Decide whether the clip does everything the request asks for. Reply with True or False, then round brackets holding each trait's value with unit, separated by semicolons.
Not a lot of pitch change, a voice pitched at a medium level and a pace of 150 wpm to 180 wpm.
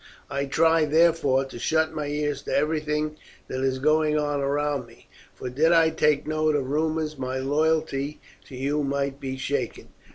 True (2.3 semitones; 145 Hz; 170 wpm)